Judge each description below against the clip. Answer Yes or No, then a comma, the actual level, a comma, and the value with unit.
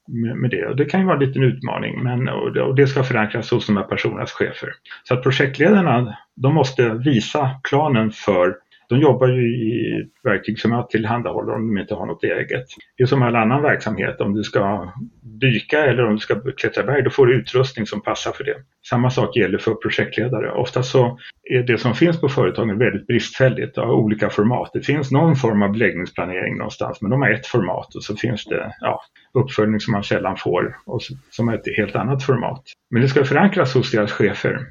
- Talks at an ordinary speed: No, fast, 210 wpm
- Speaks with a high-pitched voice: No, low, 125 Hz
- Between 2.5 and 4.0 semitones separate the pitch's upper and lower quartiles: Yes, average, 3.5 semitones